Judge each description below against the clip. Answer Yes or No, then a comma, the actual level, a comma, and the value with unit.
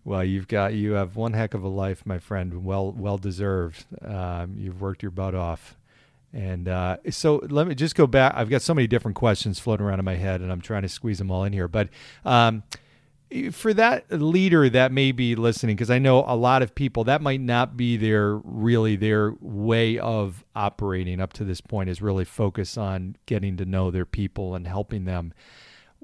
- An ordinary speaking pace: No, fast, 210 wpm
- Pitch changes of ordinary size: Yes, average, 4.1 semitones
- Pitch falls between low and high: No, low, 105 Hz